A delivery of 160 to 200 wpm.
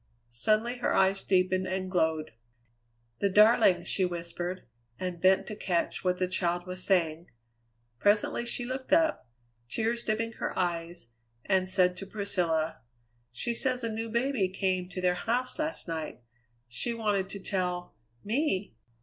No: average, 150 wpm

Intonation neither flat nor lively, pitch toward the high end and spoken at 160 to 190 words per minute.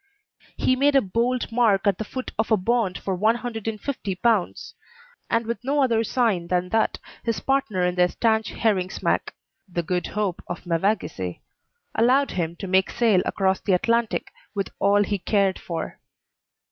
Yes: average, 4.1 semitones; high, 210 Hz; average, 165 wpm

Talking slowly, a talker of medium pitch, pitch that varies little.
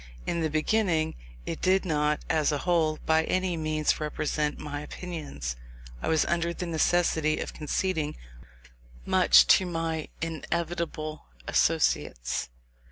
Yes: slow, 125 wpm; medium, 160 Hz; narrow, 2.1 semitones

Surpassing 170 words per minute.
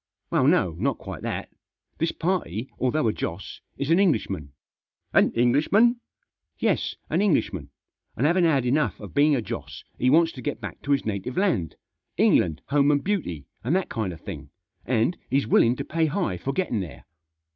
Yes: average, 190 wpm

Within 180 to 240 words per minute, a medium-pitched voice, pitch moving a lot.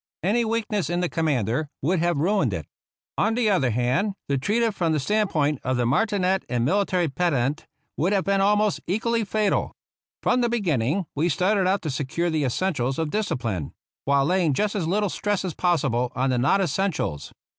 Yes: average, 195 wpm; medium, 175 Hz; wide, 6.6 semitones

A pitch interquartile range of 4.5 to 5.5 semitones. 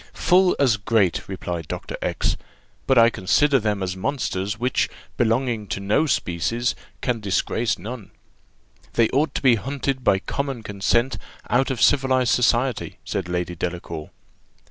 Yes: average, 5.2 semitones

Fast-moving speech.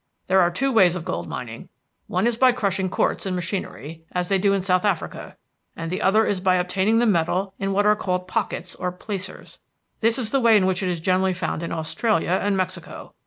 Yes: fast, 220 wpm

